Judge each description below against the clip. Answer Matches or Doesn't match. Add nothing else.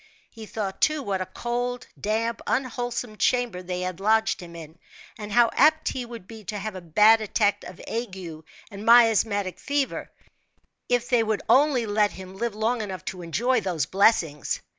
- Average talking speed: Matches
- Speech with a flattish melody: Doesn't match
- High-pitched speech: Matches